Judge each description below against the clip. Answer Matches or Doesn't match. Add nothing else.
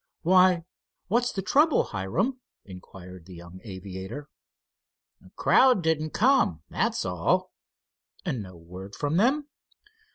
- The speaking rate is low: Matches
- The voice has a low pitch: Doesn't match